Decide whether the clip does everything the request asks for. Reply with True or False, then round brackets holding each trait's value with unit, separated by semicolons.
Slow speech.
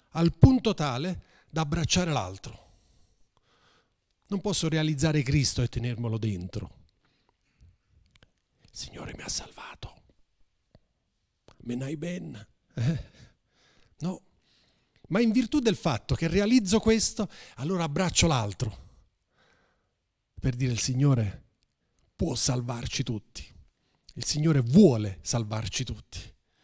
True (100 wpm)